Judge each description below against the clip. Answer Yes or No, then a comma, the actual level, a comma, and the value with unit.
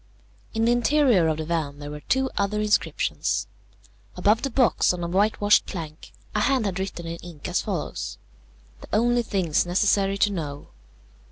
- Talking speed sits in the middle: Yes, average, 170 wpm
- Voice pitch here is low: No, high, 195 Hz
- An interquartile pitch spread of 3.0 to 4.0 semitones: No, average, 4.8 semitones